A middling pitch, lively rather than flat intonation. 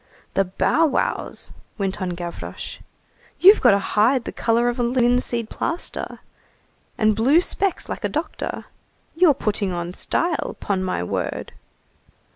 No: high, 230 Hz; wide, 5.7 semitones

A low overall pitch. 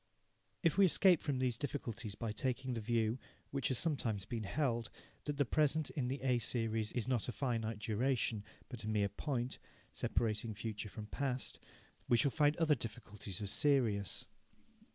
Yes: low, 120 Hz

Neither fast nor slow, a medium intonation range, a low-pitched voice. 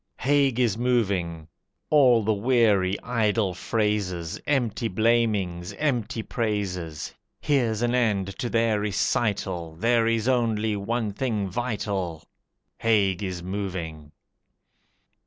No: slow, 105 wpm; average, 3.9 semitones; low, 105 Hz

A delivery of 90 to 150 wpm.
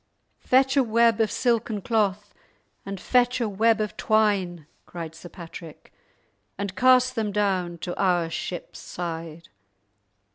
Yes: slow, 135 wpm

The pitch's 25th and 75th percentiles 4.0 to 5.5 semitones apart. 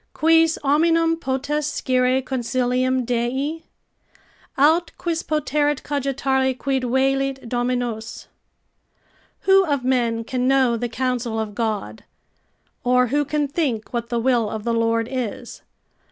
No: average, 3.2 semitones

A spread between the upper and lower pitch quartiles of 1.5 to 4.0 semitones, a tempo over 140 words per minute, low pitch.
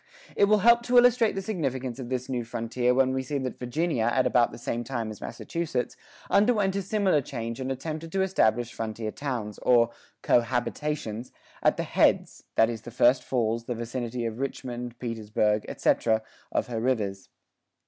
No: average, 4.5 semitones; average, 180 wpm; low, 125 Hz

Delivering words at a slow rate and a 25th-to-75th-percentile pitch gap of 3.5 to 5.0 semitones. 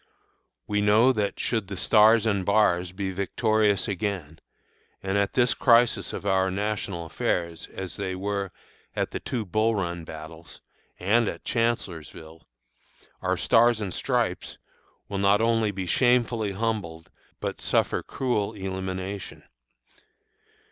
No: slow, 130 wpm; average, 2.9 semitones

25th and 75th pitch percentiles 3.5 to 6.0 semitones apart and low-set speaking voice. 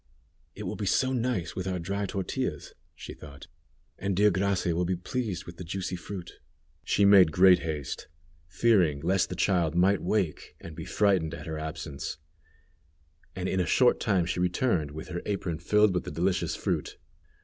No: average, 3.1 semitones; very low, 90 Hz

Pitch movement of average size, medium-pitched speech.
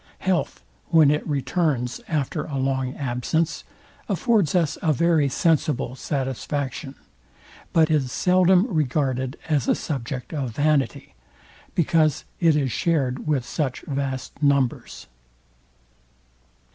Yes: average, 3.4 semitones; medium, 145 Hz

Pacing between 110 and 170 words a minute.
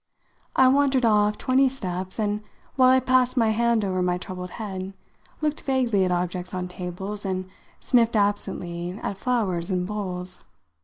Yes: average, 155 wpm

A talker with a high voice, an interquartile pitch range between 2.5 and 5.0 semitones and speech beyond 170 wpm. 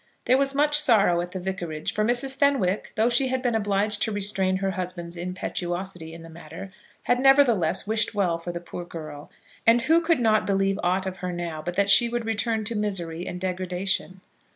Yes: high, 195 Hz; average, 4.5 semitones; average, 200 wpm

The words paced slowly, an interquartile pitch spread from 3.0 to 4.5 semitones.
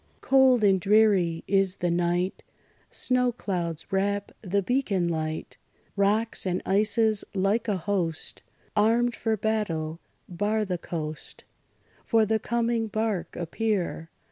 Yes: slow, 120 wpm; average, 3.9 semitones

